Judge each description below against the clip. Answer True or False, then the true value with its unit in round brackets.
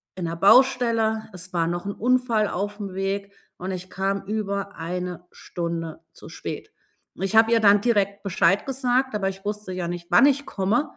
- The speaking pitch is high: True (200 Hz)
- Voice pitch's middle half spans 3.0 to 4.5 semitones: True (3.3 semitones)